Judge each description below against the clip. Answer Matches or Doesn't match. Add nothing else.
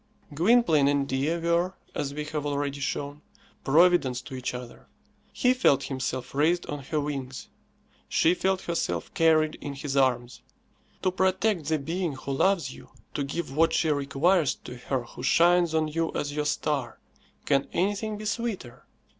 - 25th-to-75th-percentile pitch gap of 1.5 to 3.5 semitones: Doesn't match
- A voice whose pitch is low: Doesn't match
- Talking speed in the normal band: Matches